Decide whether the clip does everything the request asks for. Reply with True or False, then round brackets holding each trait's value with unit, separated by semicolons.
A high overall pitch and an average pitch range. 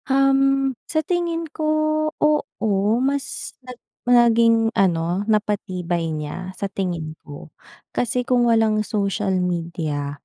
False (215 Hz; 6.4 semitones)